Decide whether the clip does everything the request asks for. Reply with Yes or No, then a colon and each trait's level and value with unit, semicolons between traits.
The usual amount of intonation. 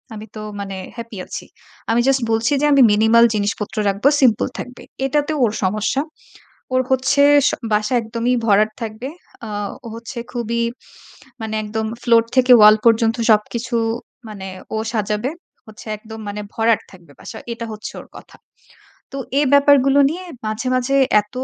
Yes: average, 3.0 semitones